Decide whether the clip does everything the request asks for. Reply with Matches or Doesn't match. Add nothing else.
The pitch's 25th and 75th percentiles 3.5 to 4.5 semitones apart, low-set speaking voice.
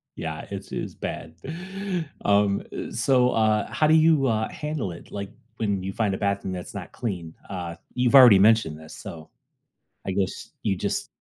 Matches